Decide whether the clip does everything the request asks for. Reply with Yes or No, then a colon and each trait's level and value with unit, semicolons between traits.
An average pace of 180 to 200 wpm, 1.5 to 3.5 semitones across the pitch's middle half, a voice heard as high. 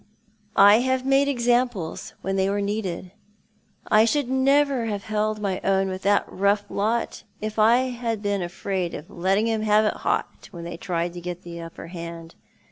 No: average, 185 wpm; average, 4.1 semitones; high, 205 Hz